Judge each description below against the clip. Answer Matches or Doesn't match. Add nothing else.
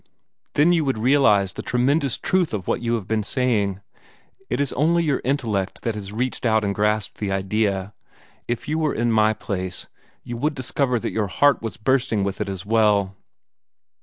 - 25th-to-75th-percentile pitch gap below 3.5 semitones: Doesn't match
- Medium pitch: Doesn't match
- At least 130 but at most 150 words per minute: Doesn't match